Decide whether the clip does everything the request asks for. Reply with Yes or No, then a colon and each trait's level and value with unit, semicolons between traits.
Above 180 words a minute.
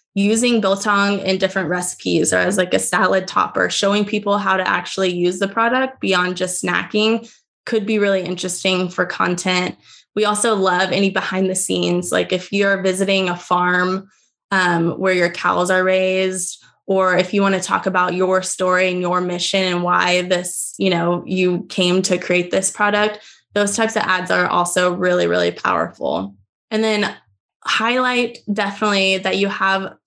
No: average, 170 wpm